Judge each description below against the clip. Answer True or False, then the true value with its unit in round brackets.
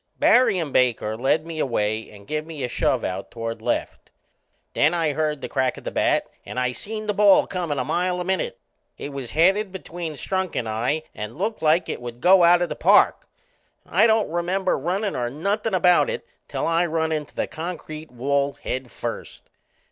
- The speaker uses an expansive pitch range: True (6.0 semitones)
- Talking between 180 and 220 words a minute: True (200 wpm)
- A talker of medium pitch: True (160 Hz)